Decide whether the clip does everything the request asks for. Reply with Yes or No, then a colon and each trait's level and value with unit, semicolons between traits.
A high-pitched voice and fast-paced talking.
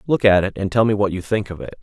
No: low, 100 Hz; fast, 360 wpm